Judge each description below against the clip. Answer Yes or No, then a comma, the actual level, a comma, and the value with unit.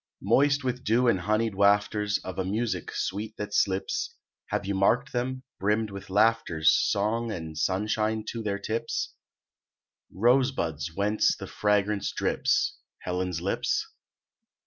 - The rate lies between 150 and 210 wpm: No, slow, 135 wpm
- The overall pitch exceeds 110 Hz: No, low, 105 Hz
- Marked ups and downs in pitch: No, average, 2.9 semitones